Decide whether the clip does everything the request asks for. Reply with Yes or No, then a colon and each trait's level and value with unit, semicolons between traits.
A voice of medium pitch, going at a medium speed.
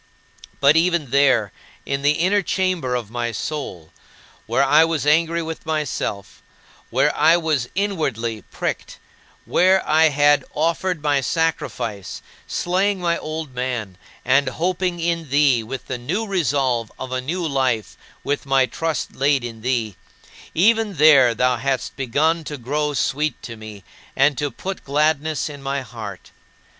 Yes: medium, 145 Hz; average, 150 wpm